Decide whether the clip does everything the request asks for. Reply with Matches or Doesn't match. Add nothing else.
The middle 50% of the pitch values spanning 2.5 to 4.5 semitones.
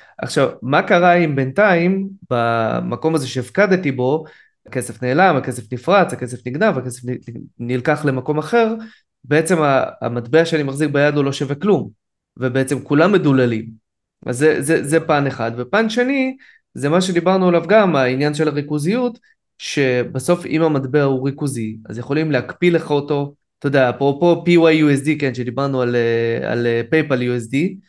Doesn't match